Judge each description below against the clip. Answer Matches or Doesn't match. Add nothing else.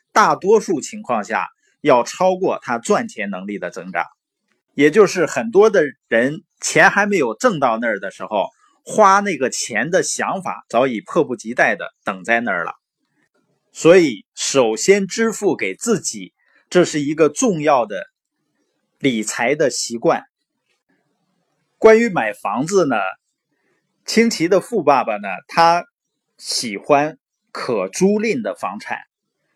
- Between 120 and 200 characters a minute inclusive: Matches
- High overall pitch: Matches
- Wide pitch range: Matches